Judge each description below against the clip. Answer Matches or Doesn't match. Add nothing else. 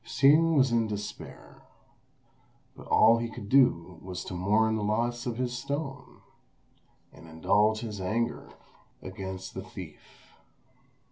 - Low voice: Matches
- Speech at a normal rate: Doesn't match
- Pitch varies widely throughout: Doesn't match